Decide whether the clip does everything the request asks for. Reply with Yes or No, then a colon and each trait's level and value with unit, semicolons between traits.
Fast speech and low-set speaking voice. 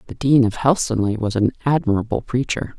No: average, 170 wpm; low, 120 Hz